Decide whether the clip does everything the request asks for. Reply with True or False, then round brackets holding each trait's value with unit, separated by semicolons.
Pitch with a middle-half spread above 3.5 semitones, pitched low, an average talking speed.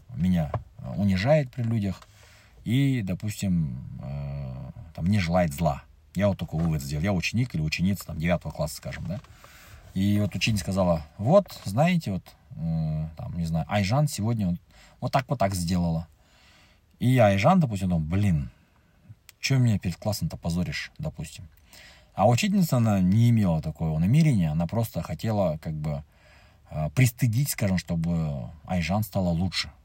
True (5.2 semitones; 95 Hz; 145 wpm)